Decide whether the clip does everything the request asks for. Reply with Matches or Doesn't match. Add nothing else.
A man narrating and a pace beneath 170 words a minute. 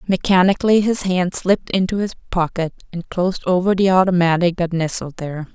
Doesn't match